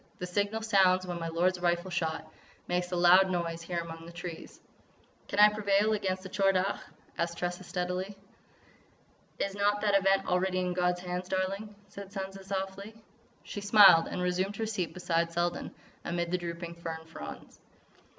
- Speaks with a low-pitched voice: No, medium, 185 Hz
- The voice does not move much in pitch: Yes, narrow, 2.1 semitones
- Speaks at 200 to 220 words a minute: No, average, 170 wpm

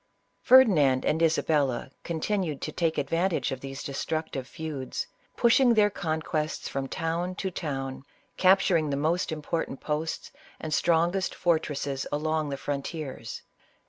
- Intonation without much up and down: No, average, 3.5 semitones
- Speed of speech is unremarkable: No, slow, 125 wpm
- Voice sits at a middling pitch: Yes, medium, 155 Hz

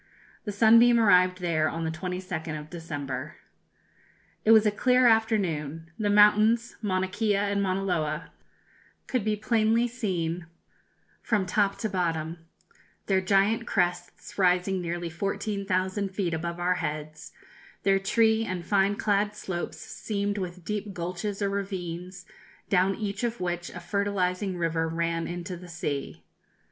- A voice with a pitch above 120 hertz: Yes, high, 190 Hz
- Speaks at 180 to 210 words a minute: No, average, 140 wpm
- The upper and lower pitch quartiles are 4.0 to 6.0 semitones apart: No, average, 3.1 semitones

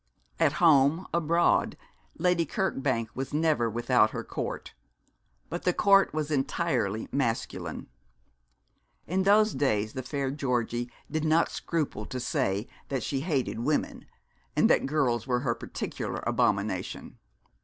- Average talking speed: No, slow, 130 wpm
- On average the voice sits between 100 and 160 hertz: Yes, medium, 140 Hz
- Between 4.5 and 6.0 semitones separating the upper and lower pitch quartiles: Yes, average, 5.2 semitones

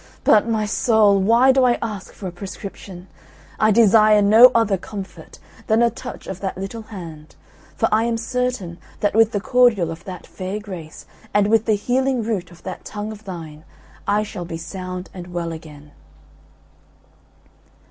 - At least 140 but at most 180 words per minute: Yes, average, 170 wpm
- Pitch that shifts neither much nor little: Yes, average, 3.7 semitones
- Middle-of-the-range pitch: No, high, 205 Hz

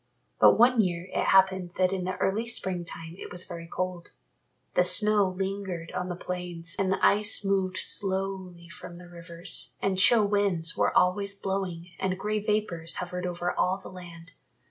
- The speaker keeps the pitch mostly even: Yes, narrow, 2.0 semitones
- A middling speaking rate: Yes, average, 175 wpm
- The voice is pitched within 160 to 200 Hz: Yes, medium, 185 Hz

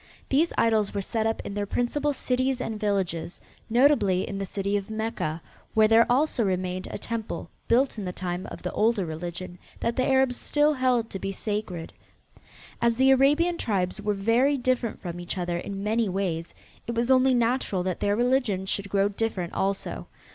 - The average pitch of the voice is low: No, high, 215 Hz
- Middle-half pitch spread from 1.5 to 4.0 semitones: No, average, 4.5 semitones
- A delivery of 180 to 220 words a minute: Yes, average, 185 wpm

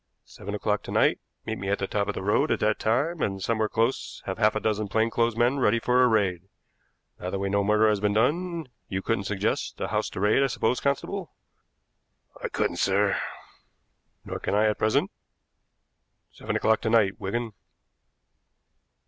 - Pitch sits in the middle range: No, low, 110 Hz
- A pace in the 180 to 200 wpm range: Yes, average, 190 wpm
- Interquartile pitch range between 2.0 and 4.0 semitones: Yes, average, 2.7 semitones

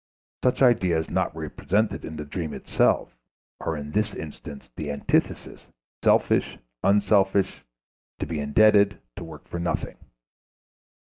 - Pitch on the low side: Yes, very low, 85 Hz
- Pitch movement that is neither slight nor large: Yes, average, 5.0 semitones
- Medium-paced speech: No, slow, 125 wpm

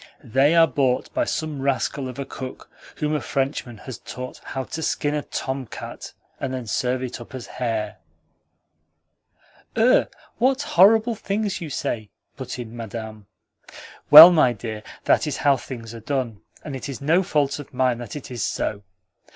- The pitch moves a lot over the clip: No, average, 3.9 semitones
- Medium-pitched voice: No, low, 130 Hz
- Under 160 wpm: No, average, 170 wpm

